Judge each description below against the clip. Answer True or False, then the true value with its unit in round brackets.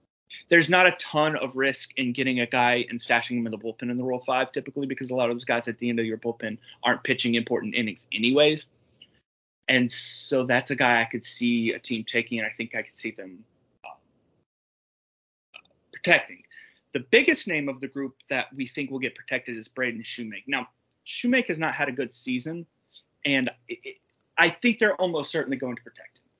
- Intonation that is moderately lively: True (4.0 semitones)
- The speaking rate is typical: False (210 wpm)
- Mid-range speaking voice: False (130 Hz)